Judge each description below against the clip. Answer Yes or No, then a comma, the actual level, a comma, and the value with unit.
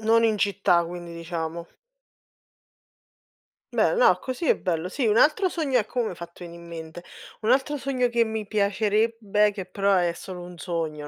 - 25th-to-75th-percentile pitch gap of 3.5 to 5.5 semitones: Yes, average, 5.0 semitones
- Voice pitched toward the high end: Yes, high, 200 Hz